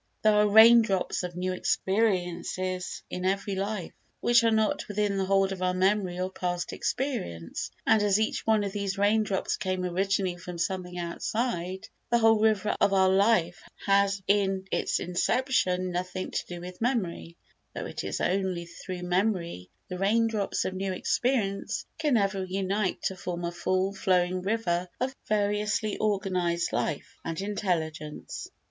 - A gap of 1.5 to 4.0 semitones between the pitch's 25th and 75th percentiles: Yes, narrow, 2.6 semitones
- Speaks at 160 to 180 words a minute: Yes, average, 165 wpm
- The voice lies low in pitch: No, high, 190 Hz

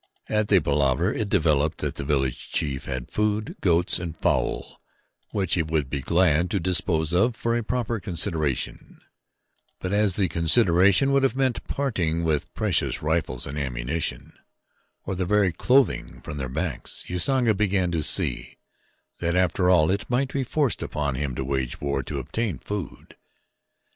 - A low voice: Yes, very low, 85 Hz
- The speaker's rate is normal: Yes, average, 165 wpm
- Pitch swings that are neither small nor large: No, wide, 5.9 semitones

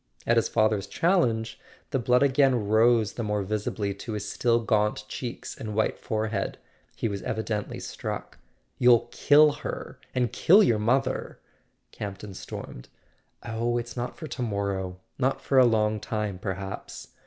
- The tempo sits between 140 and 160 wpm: Yes, average, 150 wpm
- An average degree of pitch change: Yes, average, 3.0 semitones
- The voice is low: Yes, low, 110 Hz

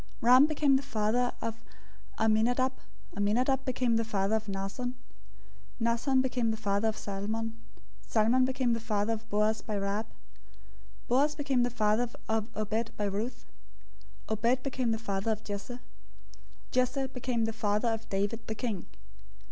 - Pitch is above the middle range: Yes, high, 225 Hz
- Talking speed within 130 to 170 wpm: Yes, average, 155 wpm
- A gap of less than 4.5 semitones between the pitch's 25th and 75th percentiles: Yes, average, 2.8 semitones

